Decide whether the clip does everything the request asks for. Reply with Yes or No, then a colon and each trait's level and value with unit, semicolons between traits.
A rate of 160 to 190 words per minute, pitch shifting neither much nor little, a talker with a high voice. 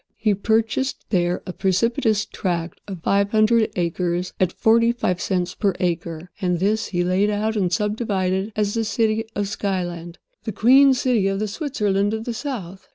Yes: average, 165 wpm; average, 3.4 semitones; high, 200 Hz